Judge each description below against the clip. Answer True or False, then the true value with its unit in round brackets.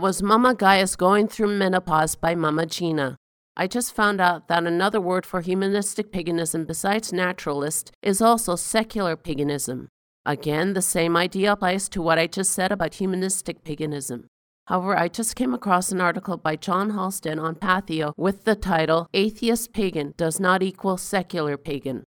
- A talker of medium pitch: True (180 Hz)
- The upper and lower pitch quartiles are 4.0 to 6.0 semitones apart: False (3.4 semitones)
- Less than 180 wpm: True (165 wpm)